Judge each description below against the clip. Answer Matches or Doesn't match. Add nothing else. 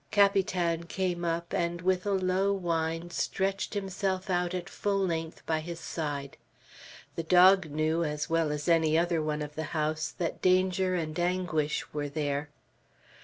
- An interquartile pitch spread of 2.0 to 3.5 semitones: Matches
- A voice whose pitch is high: Doesn't match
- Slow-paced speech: Doesn't match